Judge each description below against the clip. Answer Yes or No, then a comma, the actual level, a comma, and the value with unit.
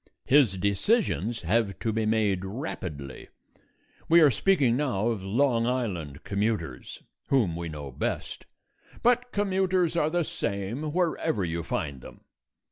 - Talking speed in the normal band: No, slow, 130 wpm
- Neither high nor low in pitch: No, low, 110 Hz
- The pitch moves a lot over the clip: Yes, wide, 8.2 semitones